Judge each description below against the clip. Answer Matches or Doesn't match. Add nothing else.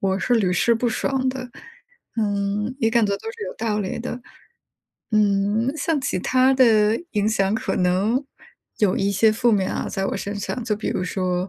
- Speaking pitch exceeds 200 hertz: Matches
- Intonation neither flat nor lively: Matches